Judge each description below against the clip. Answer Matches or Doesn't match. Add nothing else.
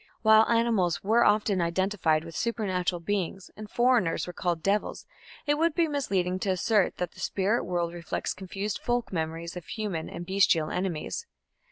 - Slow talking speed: Doesn't match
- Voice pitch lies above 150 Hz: Matches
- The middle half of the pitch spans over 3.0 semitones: Matches